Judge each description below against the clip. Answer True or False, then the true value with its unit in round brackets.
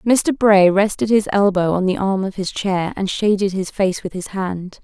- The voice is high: True (195 Hz)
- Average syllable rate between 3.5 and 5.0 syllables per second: True (4.5 syllables/s)